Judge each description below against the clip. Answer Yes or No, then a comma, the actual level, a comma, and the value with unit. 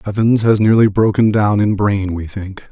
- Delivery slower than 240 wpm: Yes, average, 200 wpm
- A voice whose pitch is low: Yes, low, 105 Hz